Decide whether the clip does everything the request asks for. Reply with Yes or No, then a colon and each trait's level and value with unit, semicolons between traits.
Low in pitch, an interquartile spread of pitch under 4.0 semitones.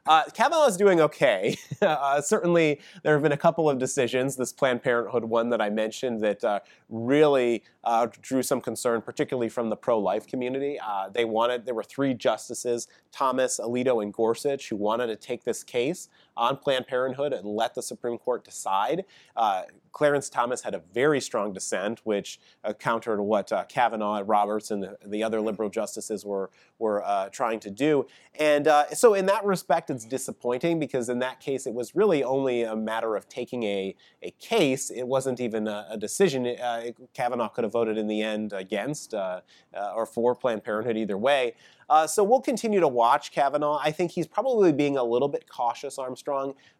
No: low, 125 Hz; average, 4.6 semitones